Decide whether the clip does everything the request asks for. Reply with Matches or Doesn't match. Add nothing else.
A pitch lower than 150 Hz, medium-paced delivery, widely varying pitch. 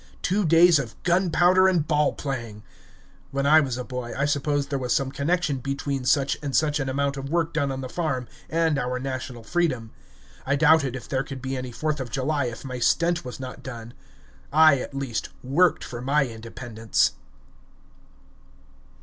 Doesn't match